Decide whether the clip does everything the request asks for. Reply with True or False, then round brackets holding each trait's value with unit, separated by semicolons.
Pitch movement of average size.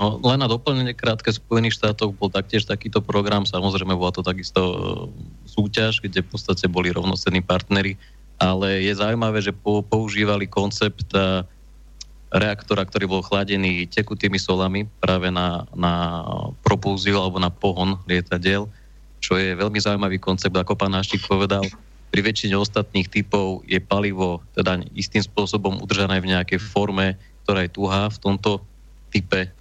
False (1.9 semitones)